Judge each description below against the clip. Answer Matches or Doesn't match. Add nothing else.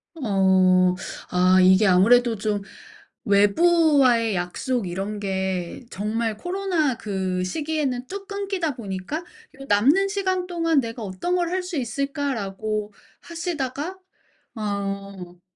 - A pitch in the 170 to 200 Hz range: Doesn't match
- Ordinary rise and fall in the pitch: Doesn't match